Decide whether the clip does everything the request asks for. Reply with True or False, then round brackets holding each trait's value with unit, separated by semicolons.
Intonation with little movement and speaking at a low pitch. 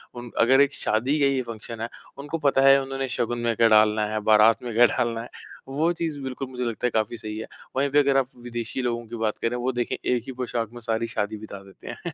False (3.1 semitones; 120 Hz)